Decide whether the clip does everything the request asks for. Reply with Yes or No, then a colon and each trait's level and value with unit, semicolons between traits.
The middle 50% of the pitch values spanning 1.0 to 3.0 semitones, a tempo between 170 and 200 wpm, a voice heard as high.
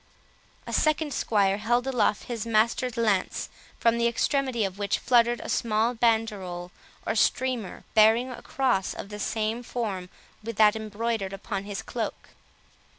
No: narrow, 2.6 semitones; average, 150 wpm; high, 225 Hz